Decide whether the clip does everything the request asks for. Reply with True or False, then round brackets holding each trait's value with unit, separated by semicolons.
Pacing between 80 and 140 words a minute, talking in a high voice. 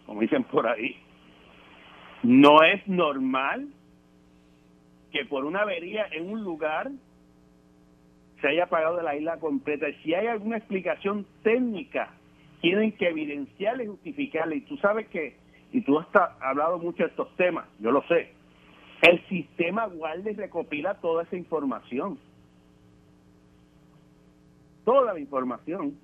False (135 wpm; 155 Hz)